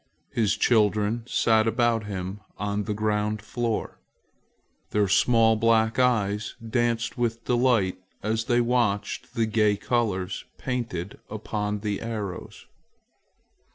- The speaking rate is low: Yes, slow, 115 wpm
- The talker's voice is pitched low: Yes, low, 110 Hz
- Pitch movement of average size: No, narrow, 2.2 semitones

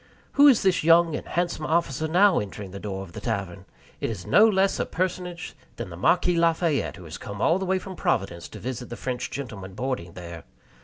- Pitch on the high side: No, low, 135 Hz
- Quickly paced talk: Yes, fast, 215 wpm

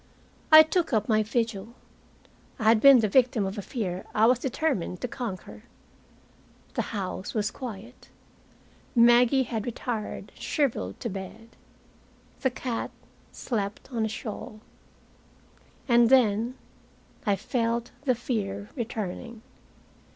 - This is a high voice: Yes, high, 230 Hz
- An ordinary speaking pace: No, slow, 120 wpm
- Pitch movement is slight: No, average, 3.0 semitones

